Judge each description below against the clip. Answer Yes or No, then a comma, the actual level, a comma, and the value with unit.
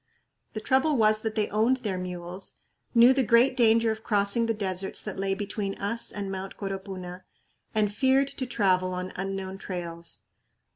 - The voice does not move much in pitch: No, average, 3.3 semitones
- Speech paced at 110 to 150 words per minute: No, average, 165 wpm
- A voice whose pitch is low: No, high, 205 Hz